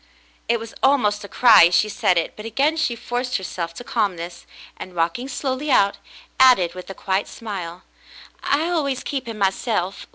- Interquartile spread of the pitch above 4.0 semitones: Yes, wide, 5.6 semitones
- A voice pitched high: Yes, high, 215 Hz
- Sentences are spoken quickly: No, average, 175 wpm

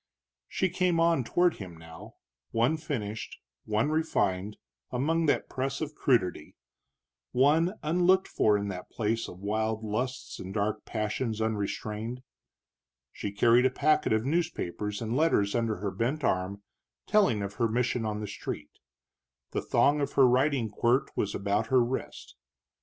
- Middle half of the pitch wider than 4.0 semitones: Yes, wide, 5.4 semitones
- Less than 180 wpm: Yes, average, 150 wpm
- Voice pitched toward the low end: Yes, low, 115 Hz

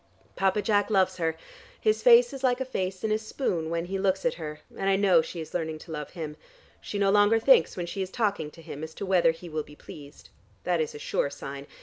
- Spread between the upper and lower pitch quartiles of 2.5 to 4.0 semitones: No, average, 4.4 semitones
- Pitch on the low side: No, medium, 185 Hz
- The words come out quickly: Yes, fast, 250 wpm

